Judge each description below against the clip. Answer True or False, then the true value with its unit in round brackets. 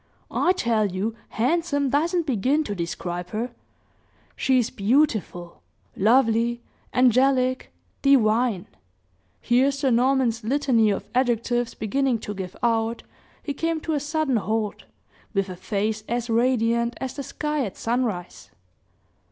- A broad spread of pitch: False (3.9 semitones)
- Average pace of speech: False (130 wpm)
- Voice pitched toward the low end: False (240 Hz)